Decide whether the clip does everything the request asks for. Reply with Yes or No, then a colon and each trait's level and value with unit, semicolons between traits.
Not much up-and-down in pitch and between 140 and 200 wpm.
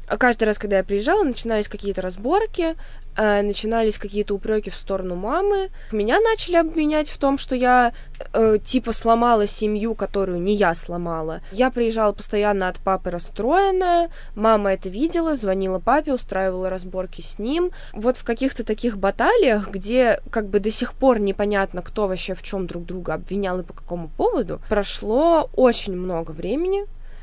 No: average, 5.1 semitones; fast, 160 wpm